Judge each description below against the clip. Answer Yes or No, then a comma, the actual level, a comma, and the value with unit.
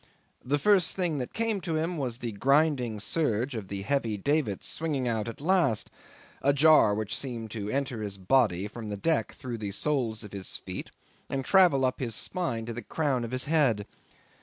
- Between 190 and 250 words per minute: Yes, average, 195 wpm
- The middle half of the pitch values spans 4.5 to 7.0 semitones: Yes, wide, 5.5 semitones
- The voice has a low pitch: Yes, low, 130 Hz